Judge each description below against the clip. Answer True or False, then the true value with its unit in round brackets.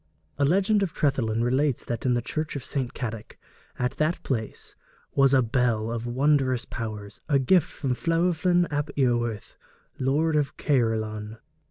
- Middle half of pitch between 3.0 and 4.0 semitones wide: False (4.4 semitones)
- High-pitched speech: False (130 Hz)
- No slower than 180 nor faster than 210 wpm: False (155 wpm)